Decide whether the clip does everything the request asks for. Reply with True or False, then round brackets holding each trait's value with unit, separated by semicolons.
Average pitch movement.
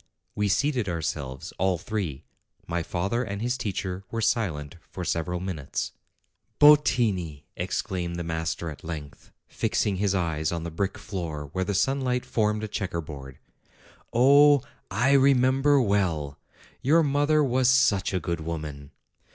False (7.1 semitones)